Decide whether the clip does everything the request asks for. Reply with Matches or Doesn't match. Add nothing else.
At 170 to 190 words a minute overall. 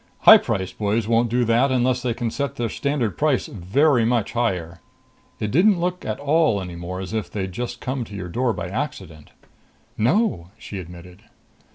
Matches